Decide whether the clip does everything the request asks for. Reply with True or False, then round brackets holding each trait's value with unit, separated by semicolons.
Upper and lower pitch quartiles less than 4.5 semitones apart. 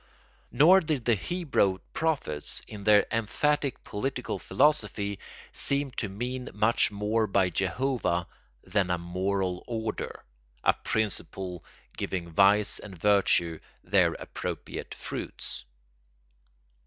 False (5.0 semitones)